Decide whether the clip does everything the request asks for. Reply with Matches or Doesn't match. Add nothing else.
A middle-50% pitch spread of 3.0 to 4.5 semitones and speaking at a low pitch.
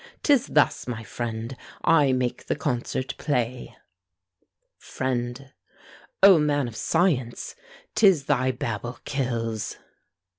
Matches